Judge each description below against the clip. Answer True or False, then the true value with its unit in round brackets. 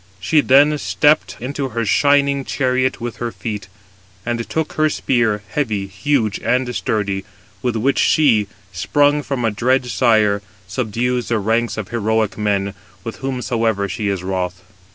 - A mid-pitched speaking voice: False (115 Hz)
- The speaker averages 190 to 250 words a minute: False (150 wpm)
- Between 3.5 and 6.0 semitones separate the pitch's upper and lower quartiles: True (4.2 semitones)